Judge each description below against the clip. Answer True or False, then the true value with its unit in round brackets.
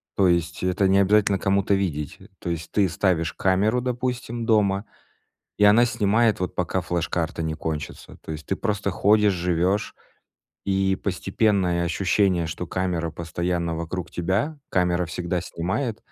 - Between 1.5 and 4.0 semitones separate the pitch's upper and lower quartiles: True (3.0 semitones)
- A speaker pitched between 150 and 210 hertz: False (95 Hz)